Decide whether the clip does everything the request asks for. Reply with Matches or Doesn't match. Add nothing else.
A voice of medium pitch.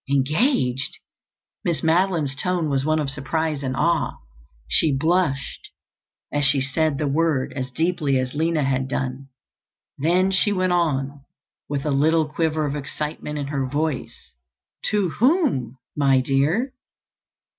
Matches